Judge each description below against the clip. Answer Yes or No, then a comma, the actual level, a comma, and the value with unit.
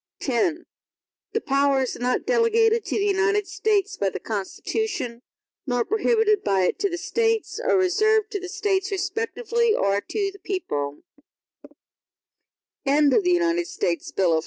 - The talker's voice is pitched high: Yes, very high, 395 Hz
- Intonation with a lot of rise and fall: Yes, wide, 8.3 semitones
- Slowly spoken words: Yes, slow, 120 wpm